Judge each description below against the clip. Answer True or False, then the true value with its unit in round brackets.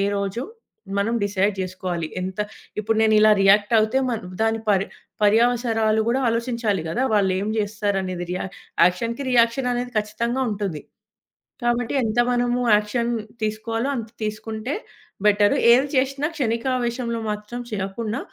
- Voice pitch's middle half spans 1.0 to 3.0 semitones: True (2.7 semitones)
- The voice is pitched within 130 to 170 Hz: False (220 Hz)